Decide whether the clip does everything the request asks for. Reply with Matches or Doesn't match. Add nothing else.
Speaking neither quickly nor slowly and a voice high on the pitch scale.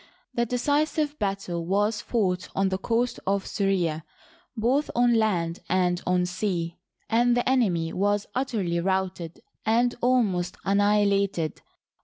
Doesn't match